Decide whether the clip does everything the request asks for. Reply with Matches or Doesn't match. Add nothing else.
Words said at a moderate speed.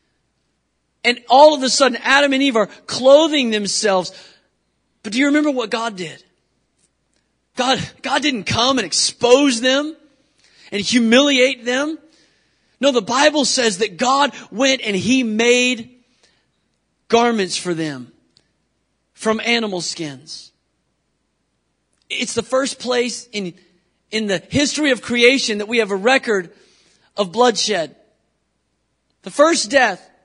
Doesn't match